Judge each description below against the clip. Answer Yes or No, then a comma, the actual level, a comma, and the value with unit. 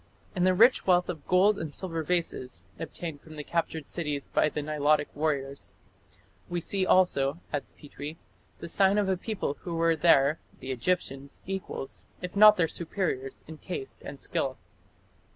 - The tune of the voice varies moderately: Yes, average, 4.0 semitones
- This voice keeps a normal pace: Yes, average, 160 wpm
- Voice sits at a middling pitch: Yes, medium, 165 Hz